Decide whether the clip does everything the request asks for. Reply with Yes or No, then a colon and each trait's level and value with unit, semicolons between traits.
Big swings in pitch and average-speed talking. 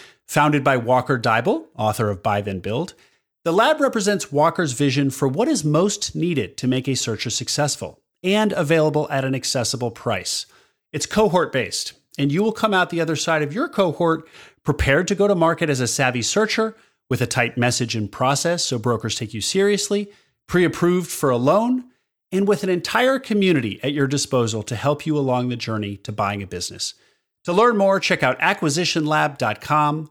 Yes: wide, 6.8 semitones; average, 185 wpm